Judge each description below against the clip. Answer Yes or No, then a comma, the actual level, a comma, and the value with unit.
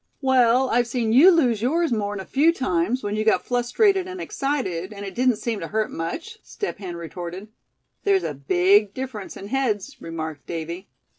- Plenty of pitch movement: Yes, wide, 6.1 semitones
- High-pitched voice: Yes, high, 220 Hz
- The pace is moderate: Yes, average, 180 wpm